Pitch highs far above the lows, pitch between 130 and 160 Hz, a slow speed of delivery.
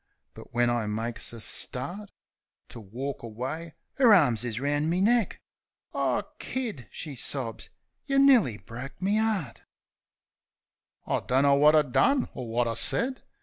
No: wide, 9.0 semitones; medium, 140 Hz; average, 155 wpm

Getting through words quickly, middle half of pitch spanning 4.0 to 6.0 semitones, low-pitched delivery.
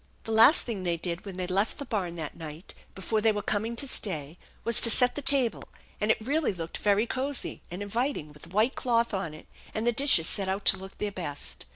No: fast, 235 wpm; average, 4.7 semitones; high, 205 Hz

